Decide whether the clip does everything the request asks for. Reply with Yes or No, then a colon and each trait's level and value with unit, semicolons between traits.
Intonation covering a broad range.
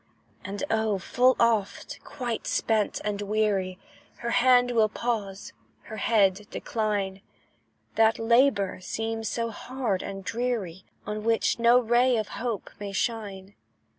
No: average, 2.8 semitones